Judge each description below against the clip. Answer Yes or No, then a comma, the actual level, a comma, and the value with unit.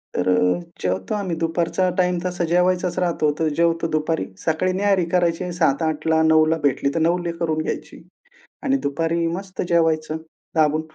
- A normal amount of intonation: No, narrow, 2.3 semitones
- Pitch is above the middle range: No, medium, 165 Hz